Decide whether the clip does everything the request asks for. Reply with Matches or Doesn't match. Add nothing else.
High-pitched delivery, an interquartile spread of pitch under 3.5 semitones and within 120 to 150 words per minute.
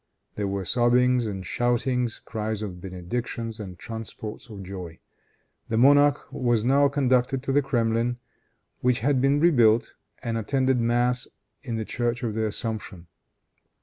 Doesn't match